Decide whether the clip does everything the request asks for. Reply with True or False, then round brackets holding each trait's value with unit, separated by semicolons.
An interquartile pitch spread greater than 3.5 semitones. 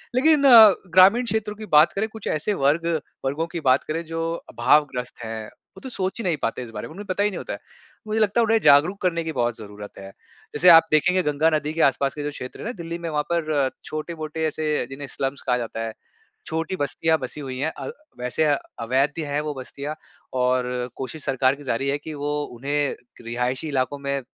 True (4.2 semitones)